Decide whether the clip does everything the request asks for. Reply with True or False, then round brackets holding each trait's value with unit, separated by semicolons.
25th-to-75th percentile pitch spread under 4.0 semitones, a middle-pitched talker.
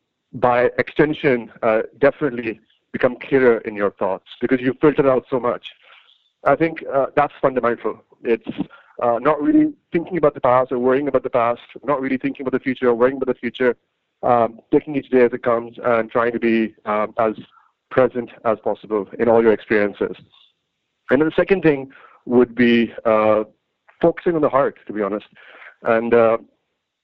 False (3.2 semitones; 125 Hz)